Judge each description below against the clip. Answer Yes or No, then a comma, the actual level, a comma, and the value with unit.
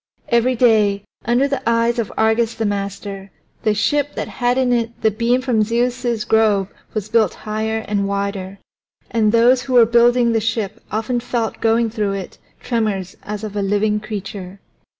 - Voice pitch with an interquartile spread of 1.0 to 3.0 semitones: Yes, narrow, 2.5 semitones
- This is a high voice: Yes, high, 220 Hz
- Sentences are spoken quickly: No, average, 170 wpm